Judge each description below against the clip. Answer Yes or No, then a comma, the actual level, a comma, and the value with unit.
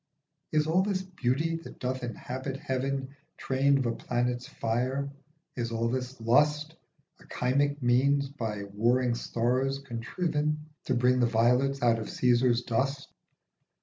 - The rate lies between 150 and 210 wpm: No, average, 140 wpm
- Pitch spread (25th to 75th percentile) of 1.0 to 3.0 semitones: Yes, average, 2.7 semitones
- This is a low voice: Yes, low, 130 Hz